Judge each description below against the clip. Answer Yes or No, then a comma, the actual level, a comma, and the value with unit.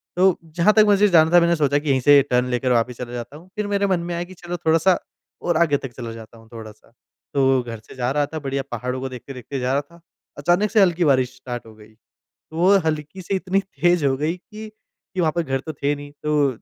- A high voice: No, medium, 150 Hz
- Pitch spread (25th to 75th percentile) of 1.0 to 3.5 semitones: No, wide, 5.4 semitones